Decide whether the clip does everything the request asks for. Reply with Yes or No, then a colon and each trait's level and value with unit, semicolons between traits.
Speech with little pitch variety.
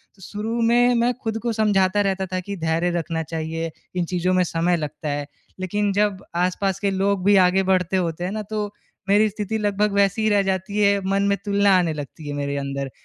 No: average, 3.2 semitones